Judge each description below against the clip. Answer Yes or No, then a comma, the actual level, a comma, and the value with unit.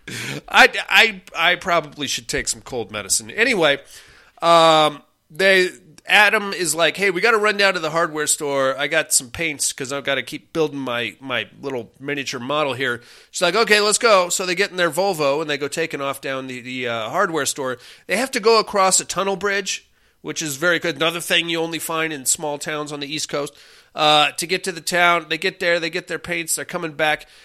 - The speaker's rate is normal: No, fast, 225 wpm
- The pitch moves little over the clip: No, average, 3.7 semitones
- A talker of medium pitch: Yes, medium, 165 Hz